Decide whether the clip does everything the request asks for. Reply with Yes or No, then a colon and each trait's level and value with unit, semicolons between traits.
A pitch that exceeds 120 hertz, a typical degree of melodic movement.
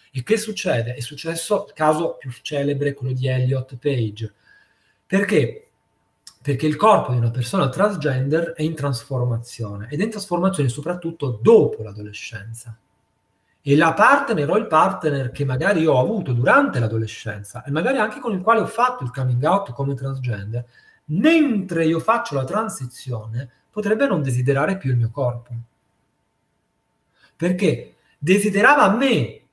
No: medium, 140 Hz; wide, 7.4 semitones